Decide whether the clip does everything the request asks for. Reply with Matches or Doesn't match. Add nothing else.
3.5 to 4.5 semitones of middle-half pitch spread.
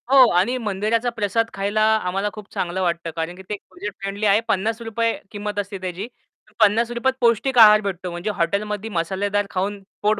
Doesn't match